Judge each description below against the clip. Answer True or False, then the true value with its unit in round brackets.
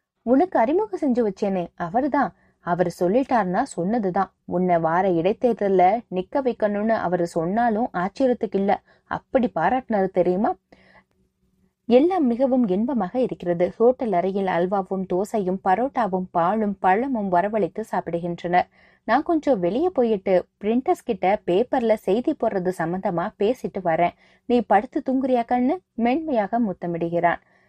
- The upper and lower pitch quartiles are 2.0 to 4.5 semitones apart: False (5.3 semitones)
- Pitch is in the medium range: False (215 Hz)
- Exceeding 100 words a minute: True (110 wpm)